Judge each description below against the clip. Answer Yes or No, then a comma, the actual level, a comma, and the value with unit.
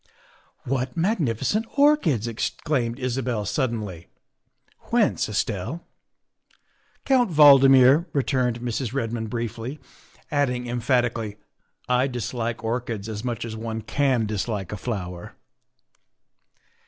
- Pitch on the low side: Yes, low, 120 Hz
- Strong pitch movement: No, average, 3.3 semitones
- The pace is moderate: No, slow, 130 wpm